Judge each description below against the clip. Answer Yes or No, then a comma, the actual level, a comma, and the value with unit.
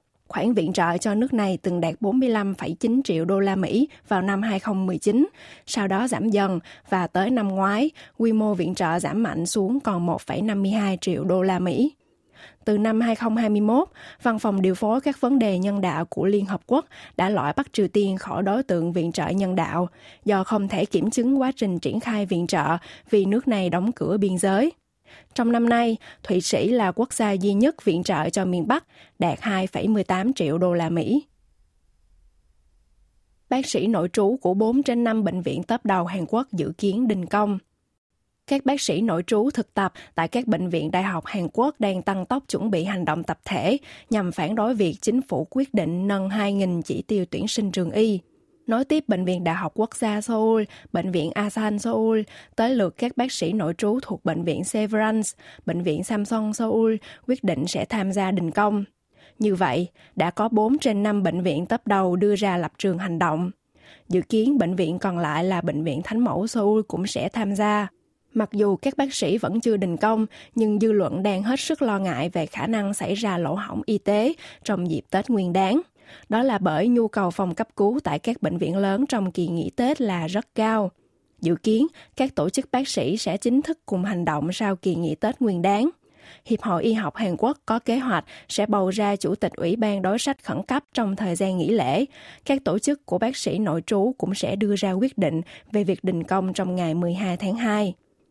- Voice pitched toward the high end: Yes, high, 205 Hz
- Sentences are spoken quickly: No, average, 210 wpm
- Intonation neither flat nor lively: Yes, average, 3.8 semitones